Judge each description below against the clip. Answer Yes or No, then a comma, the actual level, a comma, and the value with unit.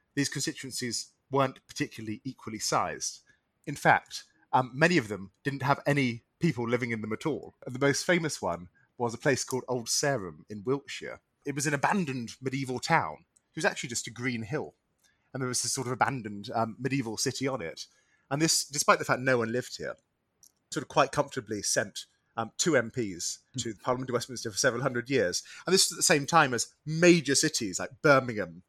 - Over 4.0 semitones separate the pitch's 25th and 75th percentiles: No, average, 3.3 semitones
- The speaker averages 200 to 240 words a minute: Yes, fast, 205 wpm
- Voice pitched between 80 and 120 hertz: No, low, 130 Hz